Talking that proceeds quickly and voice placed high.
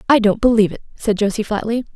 Yes: fast, 215 wpm; high, 215 Hz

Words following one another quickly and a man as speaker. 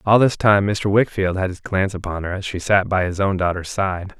Yes: fast, 260 wpm; male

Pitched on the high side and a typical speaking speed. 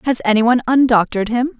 Yes: high, 240 Hz; average, 190 wpm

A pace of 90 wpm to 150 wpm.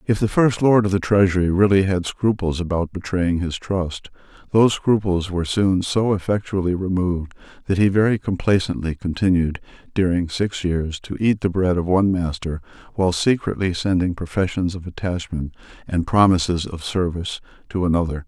No: average, 160 wpm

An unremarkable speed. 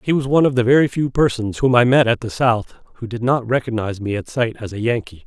No: fast, 275 wpm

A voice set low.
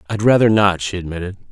Yes: very low, 95 Hz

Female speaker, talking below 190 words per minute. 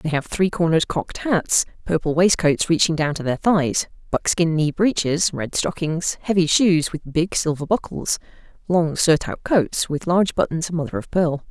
Yes: female; average, 175 wpm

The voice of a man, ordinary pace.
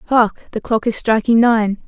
No: female; average, 190 wpm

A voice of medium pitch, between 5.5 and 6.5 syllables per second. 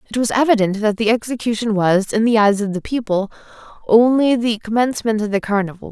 No: high, 220 Hz; 6.0 syllables/s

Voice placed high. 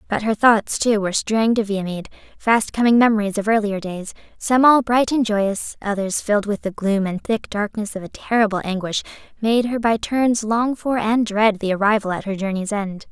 Yes: high, 215 Hz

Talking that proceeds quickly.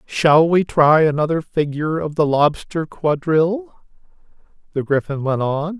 No: slow, 135 wpm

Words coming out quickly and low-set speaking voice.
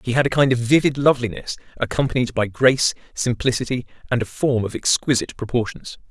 No: average, 165 wpm; low, 125 Hz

